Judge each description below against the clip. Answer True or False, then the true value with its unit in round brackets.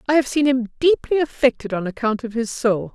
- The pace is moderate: False (225 wpm)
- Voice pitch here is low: False (245 Hz)